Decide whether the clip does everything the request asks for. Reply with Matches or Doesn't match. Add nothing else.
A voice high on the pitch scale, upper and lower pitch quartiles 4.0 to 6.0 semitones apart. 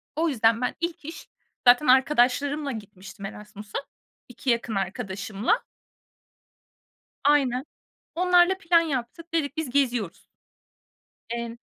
Matches